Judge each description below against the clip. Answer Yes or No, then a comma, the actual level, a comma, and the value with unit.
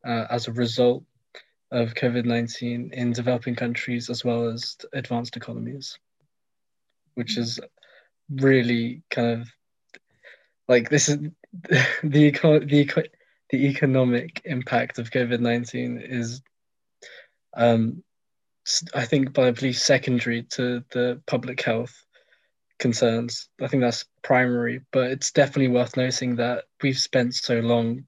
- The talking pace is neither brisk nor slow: No, slow, 120 wpm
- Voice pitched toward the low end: Yes, low, 125 Hz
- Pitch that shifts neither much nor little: No, narrow, 2.1 semitones